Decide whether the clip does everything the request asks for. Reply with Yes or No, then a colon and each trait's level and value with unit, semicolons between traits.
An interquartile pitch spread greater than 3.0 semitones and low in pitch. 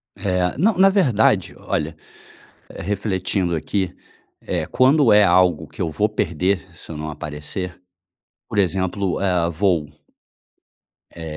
Yes: average, 3.7 semitones; very low, 95 Hz